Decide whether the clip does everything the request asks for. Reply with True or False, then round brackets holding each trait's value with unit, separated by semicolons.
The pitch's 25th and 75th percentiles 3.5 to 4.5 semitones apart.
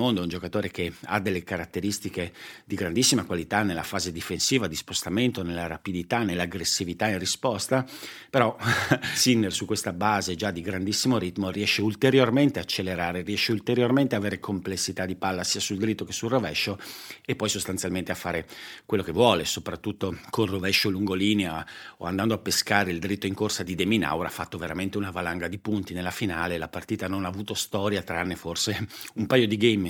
False (3.0 semitones)